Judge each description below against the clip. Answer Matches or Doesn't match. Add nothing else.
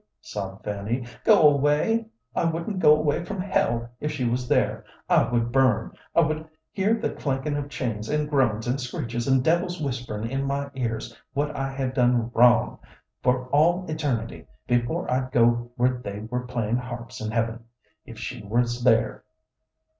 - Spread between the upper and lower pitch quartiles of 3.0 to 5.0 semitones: Matches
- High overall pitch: Doesn't match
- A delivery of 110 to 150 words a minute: Doesn't match